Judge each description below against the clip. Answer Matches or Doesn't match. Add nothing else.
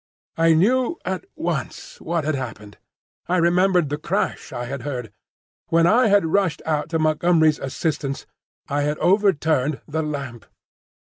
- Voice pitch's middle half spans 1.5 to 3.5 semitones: Doesn't match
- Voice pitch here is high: Doesn't match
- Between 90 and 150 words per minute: Matches